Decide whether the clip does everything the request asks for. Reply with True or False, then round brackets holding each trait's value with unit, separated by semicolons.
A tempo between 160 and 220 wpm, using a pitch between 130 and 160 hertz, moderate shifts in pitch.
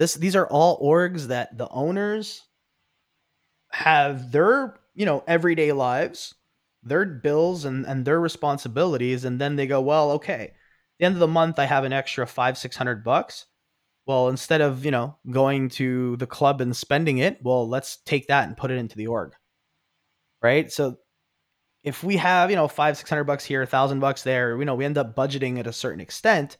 True (200 wpm; 140 Hz; 3.9 semitones)